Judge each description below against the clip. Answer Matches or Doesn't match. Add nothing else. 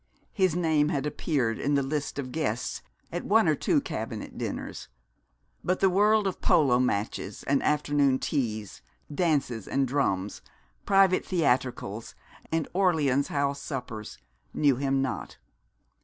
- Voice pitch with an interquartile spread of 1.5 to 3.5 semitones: Doesn't match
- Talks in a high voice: Doesn't match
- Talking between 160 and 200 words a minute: Doesn't match